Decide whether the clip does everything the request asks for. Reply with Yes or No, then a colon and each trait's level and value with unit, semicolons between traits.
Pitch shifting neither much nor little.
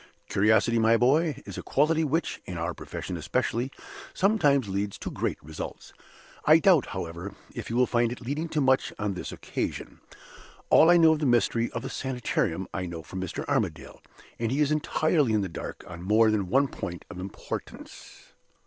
No: wide, 7.3 semitones